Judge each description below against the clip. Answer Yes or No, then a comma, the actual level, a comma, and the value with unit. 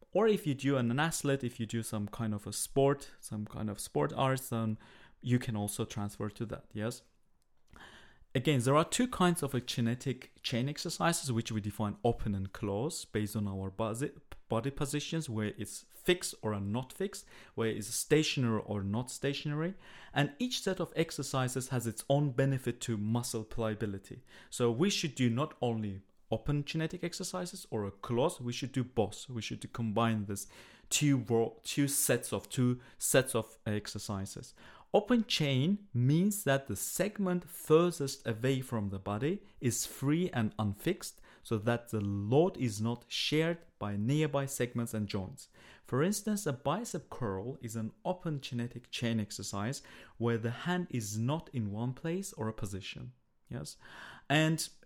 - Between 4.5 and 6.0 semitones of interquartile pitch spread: Yes, average, 5.3 semitones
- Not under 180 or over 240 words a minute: No, average, 165 wpm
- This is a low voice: Yes, low, 125 Hz